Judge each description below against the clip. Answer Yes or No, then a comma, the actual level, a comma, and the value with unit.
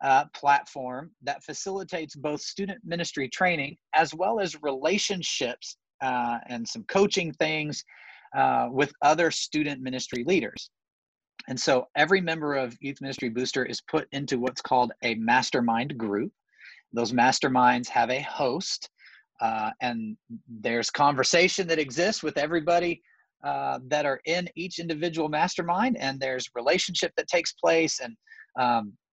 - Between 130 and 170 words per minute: Yes, average, 140 wpm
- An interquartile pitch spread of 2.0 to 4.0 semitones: No, wide, 5.5 semitones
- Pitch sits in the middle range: Yes, medium, 150 Hz